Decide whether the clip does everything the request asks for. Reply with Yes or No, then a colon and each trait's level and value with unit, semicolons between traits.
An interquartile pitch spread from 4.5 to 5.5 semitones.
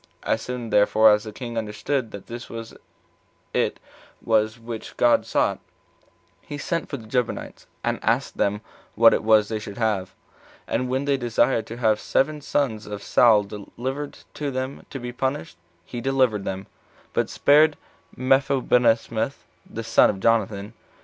No: average, 3.5 semitones